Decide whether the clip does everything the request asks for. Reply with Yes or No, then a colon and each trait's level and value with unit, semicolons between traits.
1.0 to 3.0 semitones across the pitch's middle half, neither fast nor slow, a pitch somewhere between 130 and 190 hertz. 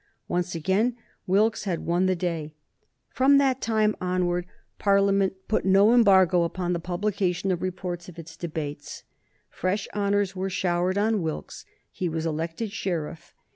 Yes: narrow, 2.6 semitones; average, 145 wpm; medium, 185 Hz